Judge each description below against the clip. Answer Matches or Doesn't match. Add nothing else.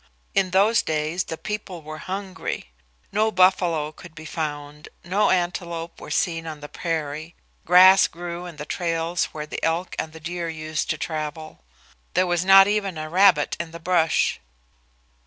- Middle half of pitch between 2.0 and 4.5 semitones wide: Matches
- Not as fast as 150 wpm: Doesn't match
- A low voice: Doesn't match